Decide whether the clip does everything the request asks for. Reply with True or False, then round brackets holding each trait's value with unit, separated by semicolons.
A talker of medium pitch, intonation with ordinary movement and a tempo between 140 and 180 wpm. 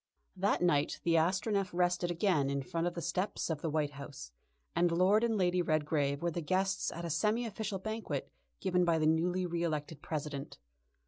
False (170 Hz; 3.2 semitones; 190 wpm)